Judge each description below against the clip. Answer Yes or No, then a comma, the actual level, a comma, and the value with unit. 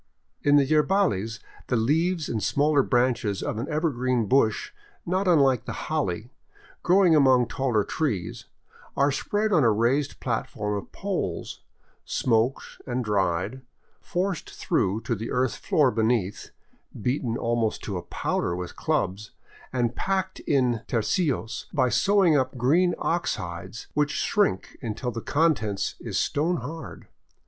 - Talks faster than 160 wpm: No, average, 140 wpm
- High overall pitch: No, low, 125 Hz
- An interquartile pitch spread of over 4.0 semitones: Yes, wide, 5.6 semitones